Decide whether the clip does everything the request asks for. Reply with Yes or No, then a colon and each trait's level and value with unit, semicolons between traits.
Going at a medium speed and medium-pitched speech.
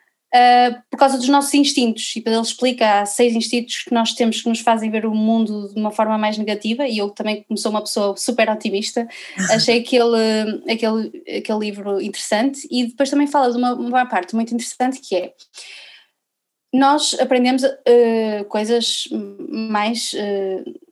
No: average, 170 wpm; high, 230 Hz